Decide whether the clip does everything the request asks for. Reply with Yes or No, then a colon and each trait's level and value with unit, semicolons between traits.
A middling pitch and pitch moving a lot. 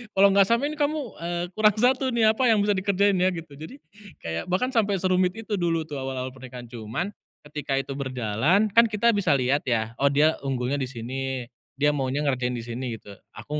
Yes: medium, 150 Hz; wide, 7.7 semitones